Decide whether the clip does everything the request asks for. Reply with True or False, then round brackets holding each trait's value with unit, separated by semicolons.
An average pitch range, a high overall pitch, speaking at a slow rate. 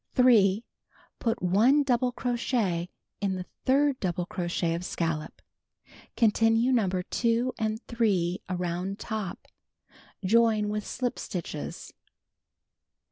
True (4.8 semitones; 215 Hz; 105 wpm)